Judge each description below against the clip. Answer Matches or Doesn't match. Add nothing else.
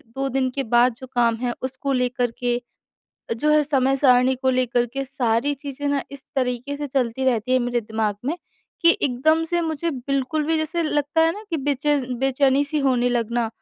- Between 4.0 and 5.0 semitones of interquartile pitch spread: Doesn't match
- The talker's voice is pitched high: Matches